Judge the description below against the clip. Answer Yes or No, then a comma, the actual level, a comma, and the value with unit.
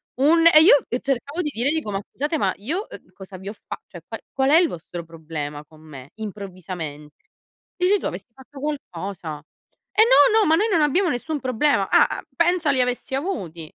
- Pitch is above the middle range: Yes, very high, 255 Hz